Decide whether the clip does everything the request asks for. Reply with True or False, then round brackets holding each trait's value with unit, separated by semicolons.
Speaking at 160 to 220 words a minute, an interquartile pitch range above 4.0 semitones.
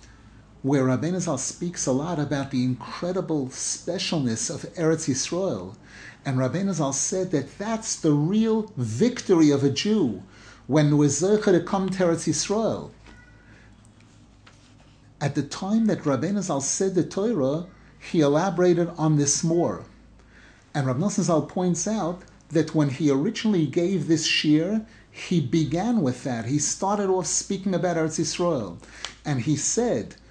False (140 wpm; 5.2 semitones)